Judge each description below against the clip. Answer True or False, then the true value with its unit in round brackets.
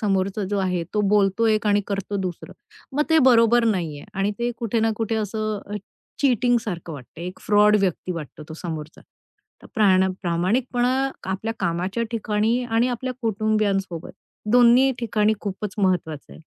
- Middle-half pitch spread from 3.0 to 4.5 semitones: True (3.6 semitones)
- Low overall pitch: False (210 Hz)